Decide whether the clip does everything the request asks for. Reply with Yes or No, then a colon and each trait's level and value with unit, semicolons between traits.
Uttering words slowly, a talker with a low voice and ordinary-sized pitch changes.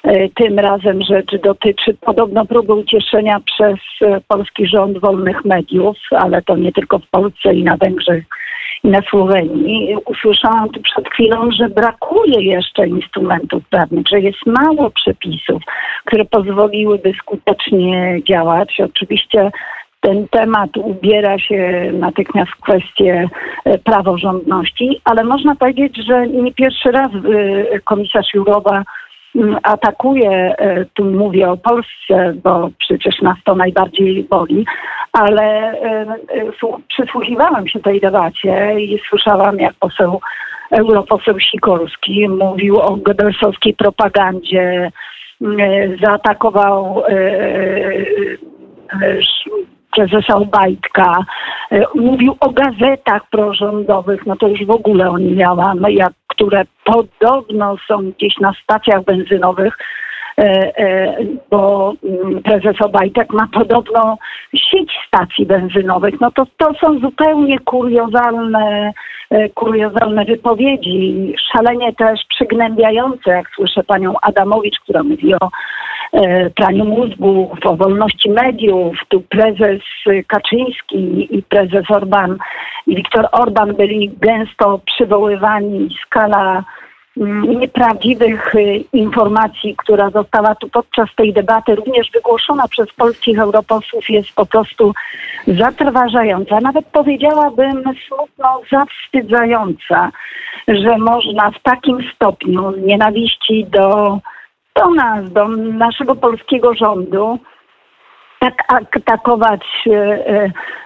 No: slow, 105 wpm; high, 210 Hz; average, 3.1 semitones